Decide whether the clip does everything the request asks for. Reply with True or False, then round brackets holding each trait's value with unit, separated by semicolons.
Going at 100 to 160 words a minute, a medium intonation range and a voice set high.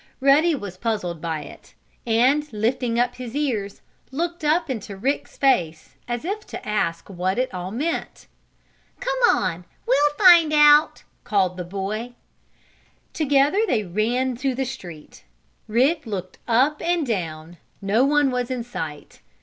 False (150 wpm; 6.9 semitones; 245 Hz)